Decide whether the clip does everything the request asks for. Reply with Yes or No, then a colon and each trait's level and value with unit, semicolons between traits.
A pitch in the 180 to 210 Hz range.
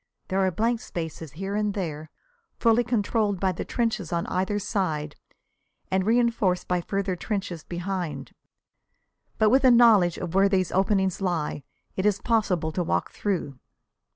Yes: high, 190 Hz